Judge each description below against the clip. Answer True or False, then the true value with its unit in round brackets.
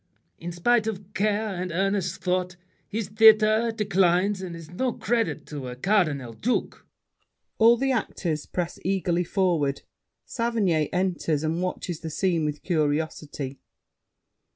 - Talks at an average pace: False (130 wpm)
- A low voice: False (185 Hz)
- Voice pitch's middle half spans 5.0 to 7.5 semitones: False (4.6 semitones)